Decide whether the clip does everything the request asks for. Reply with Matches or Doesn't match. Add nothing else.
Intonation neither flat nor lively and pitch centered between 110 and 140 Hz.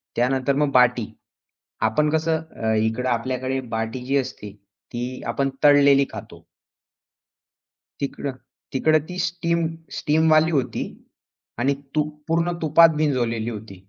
Matches